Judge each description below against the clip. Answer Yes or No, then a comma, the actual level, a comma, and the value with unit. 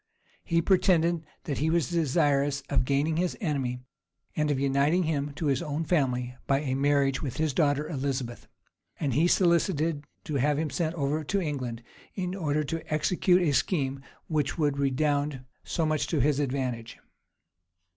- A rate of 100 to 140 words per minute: No, average, 165 wpm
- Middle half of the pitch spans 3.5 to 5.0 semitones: No, average, 2.8 semitones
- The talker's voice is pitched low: No, medium, 145 Hz